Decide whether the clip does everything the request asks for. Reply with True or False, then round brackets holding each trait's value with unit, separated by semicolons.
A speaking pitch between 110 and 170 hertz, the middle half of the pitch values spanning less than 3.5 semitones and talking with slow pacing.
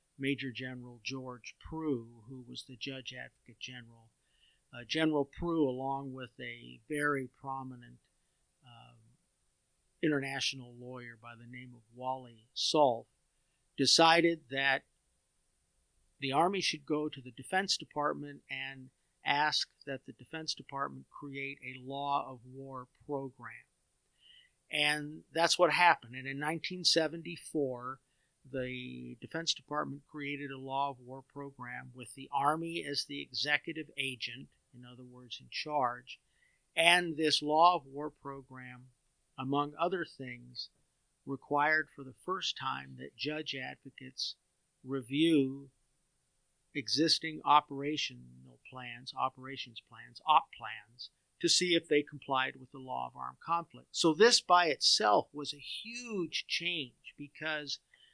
True (135 Hz; 3.0 semitones; 125 wpm)